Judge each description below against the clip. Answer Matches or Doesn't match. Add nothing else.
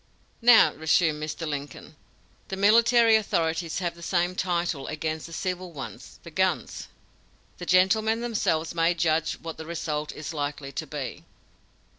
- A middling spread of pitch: Matches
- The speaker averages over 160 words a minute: Doesn't match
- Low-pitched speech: Doesn't match